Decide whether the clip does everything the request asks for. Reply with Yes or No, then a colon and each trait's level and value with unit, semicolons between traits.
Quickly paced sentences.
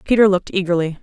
No: average, 175 wpm